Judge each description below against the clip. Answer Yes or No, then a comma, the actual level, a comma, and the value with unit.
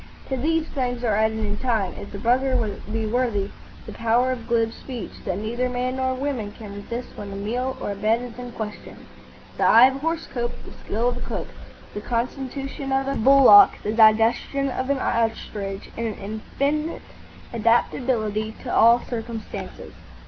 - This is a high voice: Yes, high, 235 Hz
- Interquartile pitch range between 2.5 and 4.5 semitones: Yes, average, 3.0 semitones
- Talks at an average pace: Yes, average, 180 wpm